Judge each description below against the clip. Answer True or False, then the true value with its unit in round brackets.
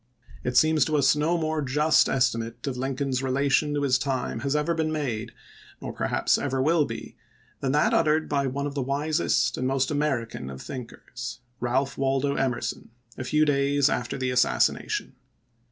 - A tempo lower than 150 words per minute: False (185 wpm)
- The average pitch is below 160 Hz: True (135 Hz)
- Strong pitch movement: False (2.8 semitones)